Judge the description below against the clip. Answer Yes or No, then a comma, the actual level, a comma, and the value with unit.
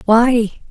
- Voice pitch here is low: No, high, 230 Hz